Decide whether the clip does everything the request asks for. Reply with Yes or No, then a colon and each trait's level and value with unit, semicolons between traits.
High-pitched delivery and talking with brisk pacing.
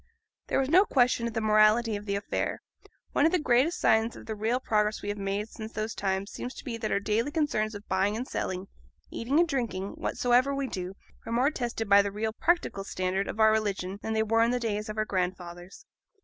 Yes: high, 220 Hz; fast, 230 wpm